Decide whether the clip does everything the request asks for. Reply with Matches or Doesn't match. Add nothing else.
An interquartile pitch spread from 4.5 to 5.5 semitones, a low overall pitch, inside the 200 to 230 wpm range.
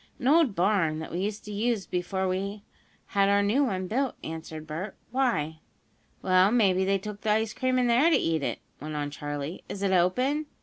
Doesn't match